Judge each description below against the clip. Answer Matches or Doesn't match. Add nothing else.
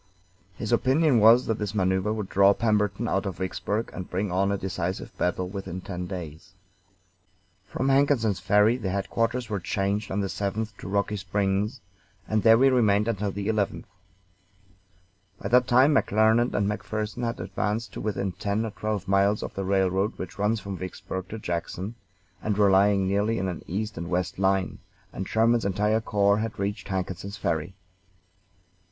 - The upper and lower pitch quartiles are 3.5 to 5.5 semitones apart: Doesn't match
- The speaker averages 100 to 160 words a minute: Doesn't match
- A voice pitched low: Matches